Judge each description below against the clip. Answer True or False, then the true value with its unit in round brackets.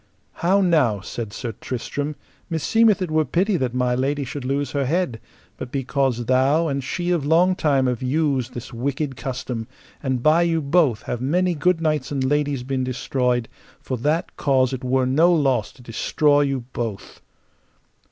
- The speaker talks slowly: False (170 wpm)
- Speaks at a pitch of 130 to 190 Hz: True (135 Hz)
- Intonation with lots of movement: False (3.8 semitones)